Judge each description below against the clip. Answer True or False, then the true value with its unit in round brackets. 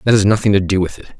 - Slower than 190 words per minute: False (350 wpm)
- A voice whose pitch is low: True (100 Hz)